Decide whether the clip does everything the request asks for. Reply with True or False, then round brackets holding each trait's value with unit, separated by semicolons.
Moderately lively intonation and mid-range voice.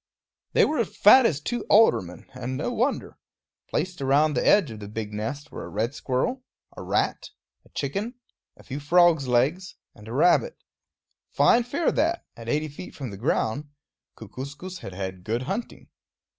False (8.9 semitones; 145 Hz)